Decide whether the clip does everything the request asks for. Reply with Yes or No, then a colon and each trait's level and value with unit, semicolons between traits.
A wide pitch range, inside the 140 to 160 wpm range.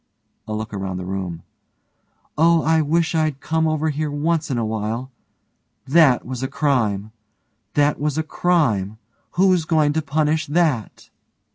Yes: wide, 6.1 semitones; average, 150 wpm